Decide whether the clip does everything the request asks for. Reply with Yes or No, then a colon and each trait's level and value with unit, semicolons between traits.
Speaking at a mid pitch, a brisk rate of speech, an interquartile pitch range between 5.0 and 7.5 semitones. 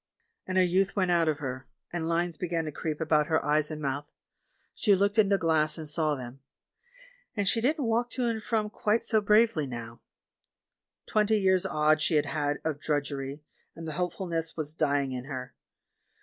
No: medium, 165 Hz; average, 195 wpm; wide, 5.5 semitones